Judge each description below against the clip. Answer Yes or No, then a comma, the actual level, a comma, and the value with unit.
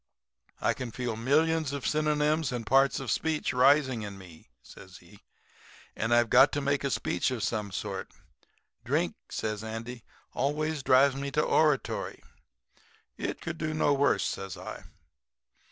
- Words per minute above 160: No, average, 155 wpm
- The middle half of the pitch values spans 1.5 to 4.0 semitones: No, average, 4.7 semitones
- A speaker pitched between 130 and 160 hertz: Yes, low, 135 Hz